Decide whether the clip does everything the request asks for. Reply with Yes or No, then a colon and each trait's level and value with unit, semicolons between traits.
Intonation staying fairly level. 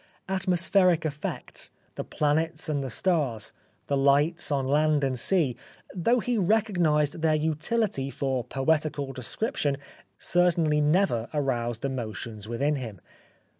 No: average, 4.2 semitones